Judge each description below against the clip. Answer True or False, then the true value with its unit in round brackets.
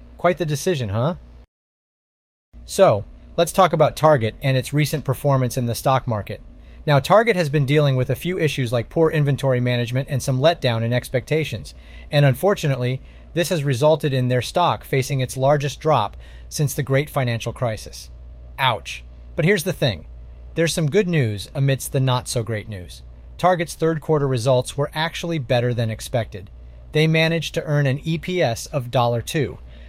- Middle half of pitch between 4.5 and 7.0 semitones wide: True (5.4 semitones)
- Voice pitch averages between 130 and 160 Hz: True (135 Hz)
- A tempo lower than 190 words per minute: True (170 wpm)